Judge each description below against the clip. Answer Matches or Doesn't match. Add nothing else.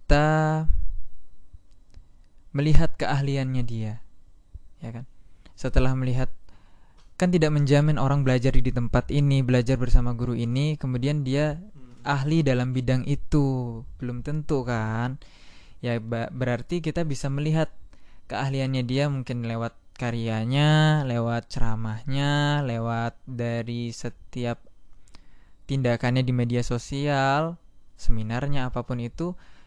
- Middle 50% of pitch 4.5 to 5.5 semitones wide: Doesn't match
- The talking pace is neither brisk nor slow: Matches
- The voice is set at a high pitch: Doesn't match